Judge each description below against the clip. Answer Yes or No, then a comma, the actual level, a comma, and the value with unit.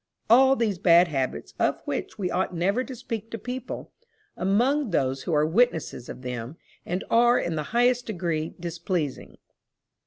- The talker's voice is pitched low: No, medium, 185 Hz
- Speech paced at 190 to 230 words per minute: No, average, 160 wpm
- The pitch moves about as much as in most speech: No, wide, 6.8 semitones